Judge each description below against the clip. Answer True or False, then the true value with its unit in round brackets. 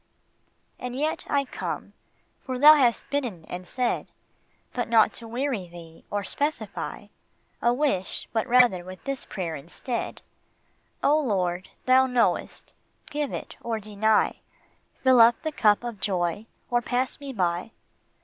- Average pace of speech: True (145 wpm)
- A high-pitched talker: True (235 Hz)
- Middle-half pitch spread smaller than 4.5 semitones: False (5.4 semitones)